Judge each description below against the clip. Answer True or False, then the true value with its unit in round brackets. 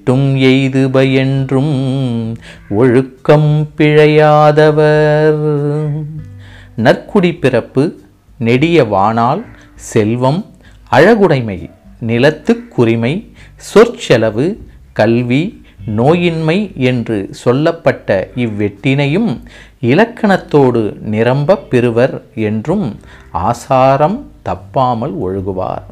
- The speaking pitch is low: True (130 Hz)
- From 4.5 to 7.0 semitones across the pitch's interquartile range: True (5.3 semitones)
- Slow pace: True (55 wpm)